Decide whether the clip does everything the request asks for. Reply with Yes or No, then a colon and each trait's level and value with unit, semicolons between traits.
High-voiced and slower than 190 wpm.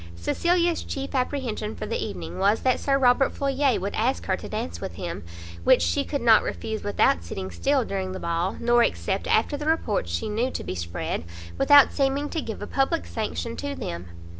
No: high, 225 Hz; average, 200 wpm